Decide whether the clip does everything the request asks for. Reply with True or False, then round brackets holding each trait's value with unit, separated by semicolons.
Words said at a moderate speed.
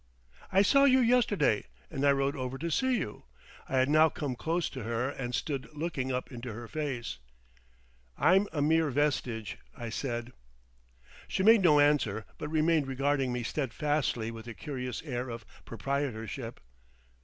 True (160 wpm)